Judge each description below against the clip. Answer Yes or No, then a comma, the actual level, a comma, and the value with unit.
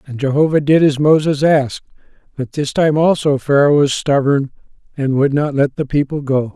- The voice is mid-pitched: Yes, medium, 145 Hz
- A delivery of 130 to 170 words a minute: No, average, 185 wpm